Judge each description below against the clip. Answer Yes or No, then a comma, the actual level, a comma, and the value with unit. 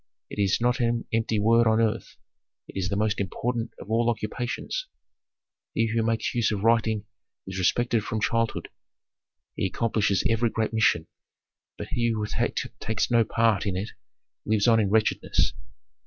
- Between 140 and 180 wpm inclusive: Yes, average, 160 wpm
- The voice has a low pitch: Yes, low, 110 Hz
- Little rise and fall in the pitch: Yes, narrow, 1.7 semitones